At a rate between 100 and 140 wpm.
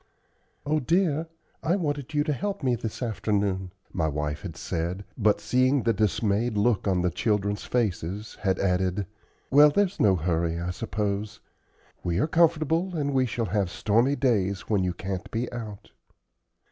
No: average, 160 wpm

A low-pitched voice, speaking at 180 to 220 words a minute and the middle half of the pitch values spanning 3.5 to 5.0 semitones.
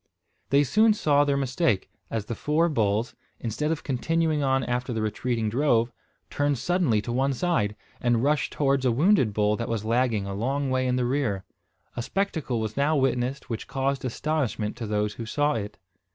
Yes: low, 130 Hz; average, 185 wpm; average, 4.3 semitones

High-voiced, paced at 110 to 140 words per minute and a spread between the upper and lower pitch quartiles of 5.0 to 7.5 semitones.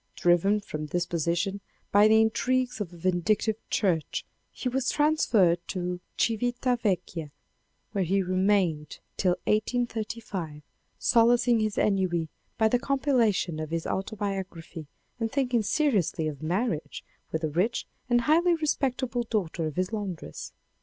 Yes: high, 205 Hz; slow, 135 wpm; wide, 5.5 semitones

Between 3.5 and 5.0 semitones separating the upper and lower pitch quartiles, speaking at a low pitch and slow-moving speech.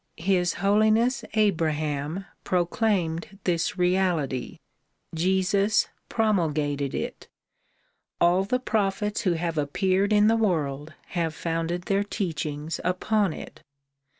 No: average, 4.0 semitones; medium, 180 Hz; slow, 100 wpm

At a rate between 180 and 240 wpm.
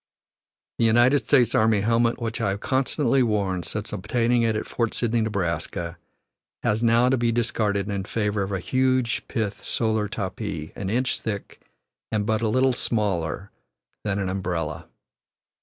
No: average, 155 wpm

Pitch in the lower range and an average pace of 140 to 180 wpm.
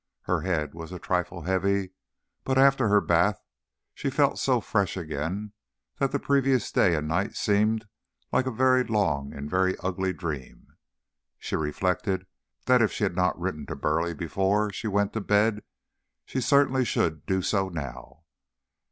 Yes: very low, 95 Hz; average, 160 wpm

